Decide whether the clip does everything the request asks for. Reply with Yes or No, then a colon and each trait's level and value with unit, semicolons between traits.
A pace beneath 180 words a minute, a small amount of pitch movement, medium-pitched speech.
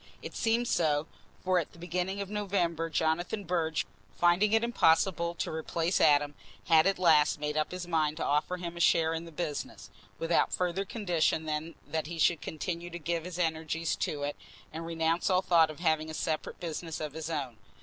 No: average, 195 wpm; narrow, 2.1 semitones; medium, 165 Hz